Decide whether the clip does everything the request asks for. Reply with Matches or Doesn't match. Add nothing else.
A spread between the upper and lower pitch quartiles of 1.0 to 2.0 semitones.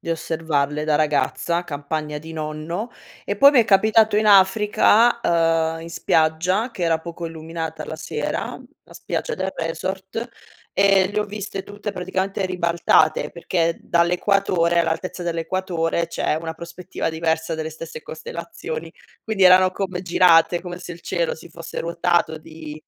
Doesn't match